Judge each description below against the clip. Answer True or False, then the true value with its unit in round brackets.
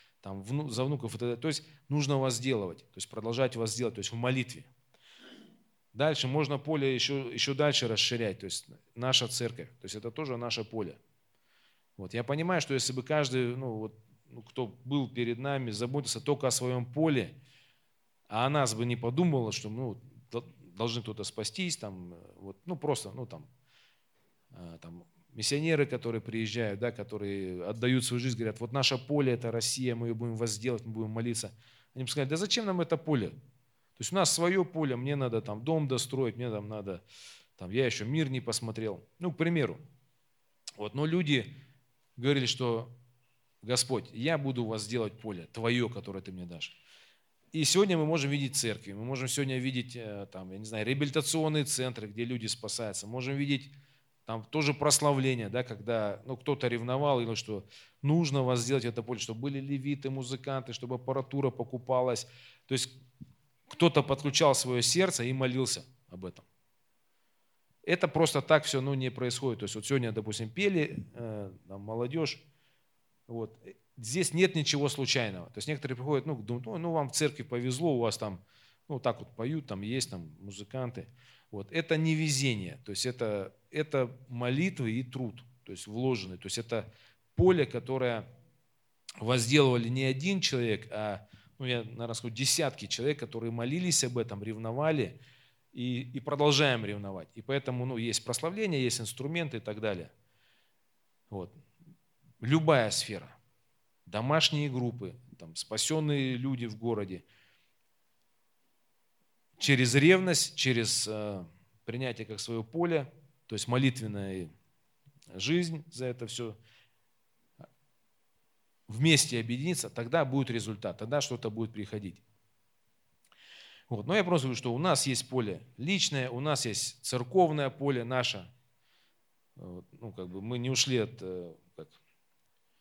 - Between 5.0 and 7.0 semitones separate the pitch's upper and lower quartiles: False (3.9 semitones)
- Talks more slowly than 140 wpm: False (155 wpm)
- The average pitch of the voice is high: False (125 Hz)